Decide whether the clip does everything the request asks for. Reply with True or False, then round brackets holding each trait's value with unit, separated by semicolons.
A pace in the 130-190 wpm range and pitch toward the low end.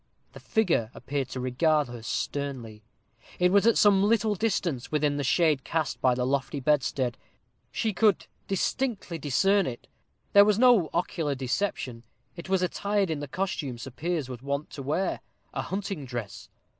False (170 wpm; 155 Hz)